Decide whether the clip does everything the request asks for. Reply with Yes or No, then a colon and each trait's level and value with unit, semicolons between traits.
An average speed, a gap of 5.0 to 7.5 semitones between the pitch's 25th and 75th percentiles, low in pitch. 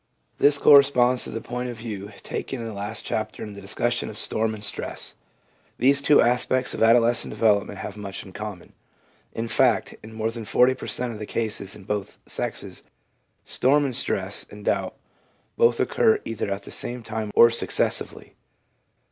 No: average, 180 wpm; average, 3.0 semitones; low, 115 Hz